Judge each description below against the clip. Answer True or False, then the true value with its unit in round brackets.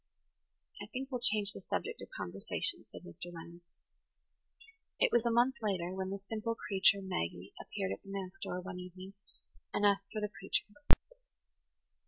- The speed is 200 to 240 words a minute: False (165 wpm)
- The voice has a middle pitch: False (195 Hz)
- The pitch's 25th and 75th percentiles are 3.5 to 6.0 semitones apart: False (2.8 semitones)